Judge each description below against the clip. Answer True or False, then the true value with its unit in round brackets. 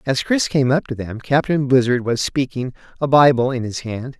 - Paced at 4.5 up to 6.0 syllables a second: True (5.0 syllables/s)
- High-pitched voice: False (130 Hz)